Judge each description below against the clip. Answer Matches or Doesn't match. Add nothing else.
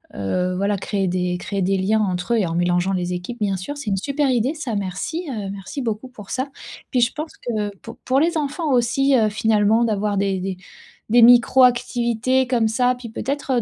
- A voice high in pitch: Matches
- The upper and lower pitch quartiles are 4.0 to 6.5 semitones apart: Matches